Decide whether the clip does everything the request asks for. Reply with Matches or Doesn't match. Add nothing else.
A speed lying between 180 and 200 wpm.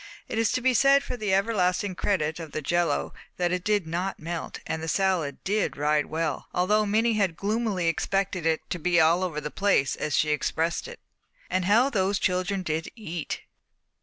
Matches